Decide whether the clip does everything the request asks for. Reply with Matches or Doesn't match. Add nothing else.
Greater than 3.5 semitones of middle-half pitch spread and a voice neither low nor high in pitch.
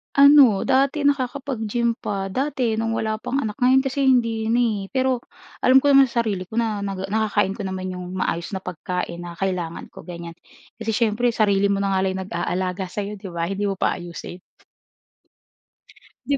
Doesn't match